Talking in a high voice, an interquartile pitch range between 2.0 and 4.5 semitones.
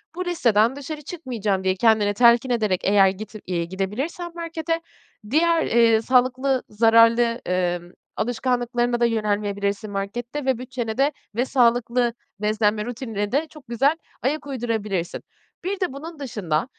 Yes: high, 235 Hz; average, 4.2 semitones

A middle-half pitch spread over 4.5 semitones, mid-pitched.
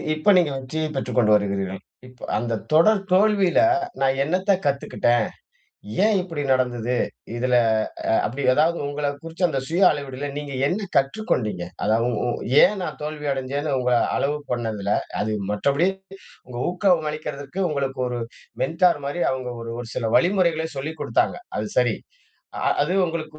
Yes: average, 5.1 semitones; medium, 145 Hz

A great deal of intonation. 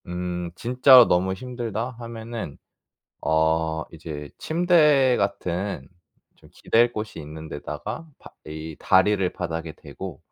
Yes: wide, 6.8 semitones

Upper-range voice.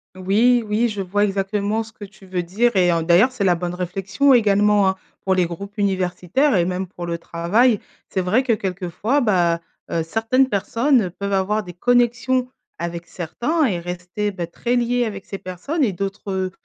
Yes: high, 200 Hz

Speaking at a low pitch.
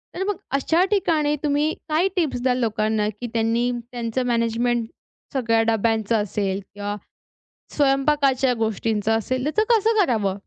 No: high, 245 Hz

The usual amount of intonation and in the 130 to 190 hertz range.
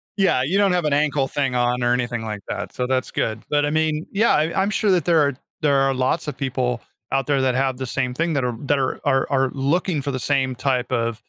Yes: average, 3.1 semitones; low, 135 Hz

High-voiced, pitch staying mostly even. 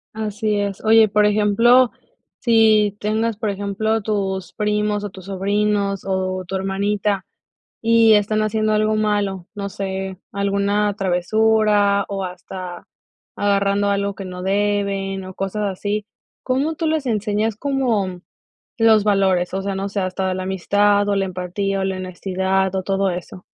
Yes: high, 200 Hz; narrow, 1.8 semitones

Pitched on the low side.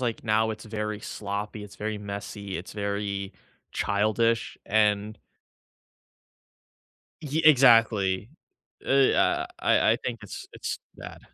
Yes: low, 105 Hz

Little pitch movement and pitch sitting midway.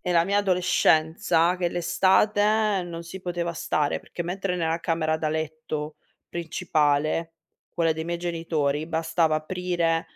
Yes: narrow, 2.2 semitones; medium, 170 Hz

